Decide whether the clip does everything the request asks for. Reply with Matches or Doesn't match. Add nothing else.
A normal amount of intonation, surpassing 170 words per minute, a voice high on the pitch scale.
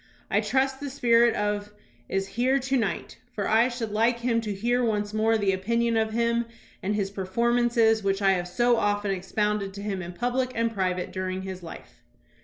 Matches